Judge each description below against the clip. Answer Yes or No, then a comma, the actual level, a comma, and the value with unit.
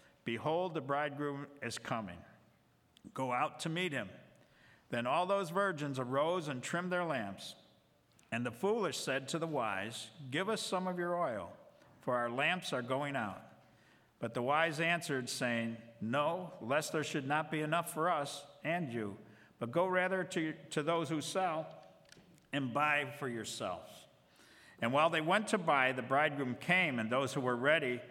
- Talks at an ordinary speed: Yes, average, 170 wpm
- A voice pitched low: No, medium, 150 Hz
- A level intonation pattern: No, average, 4.8 semitones